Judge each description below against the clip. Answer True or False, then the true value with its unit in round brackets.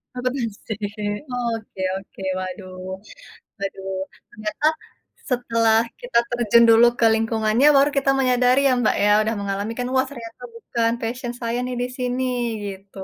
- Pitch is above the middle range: True (230 Hz)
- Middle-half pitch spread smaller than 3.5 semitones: True (2.9 semitones)